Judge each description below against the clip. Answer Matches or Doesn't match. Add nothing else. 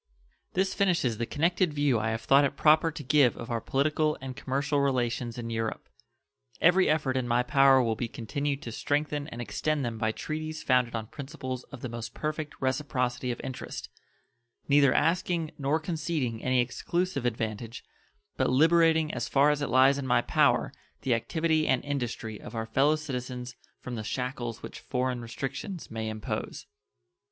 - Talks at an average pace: Matches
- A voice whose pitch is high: Doesn't match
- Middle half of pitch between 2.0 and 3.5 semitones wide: Doesn't match